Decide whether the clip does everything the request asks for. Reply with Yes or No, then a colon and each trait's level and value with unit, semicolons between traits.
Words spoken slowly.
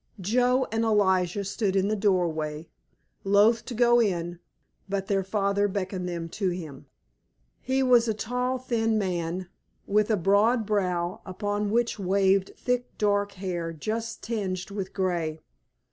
No: average, 145 wpm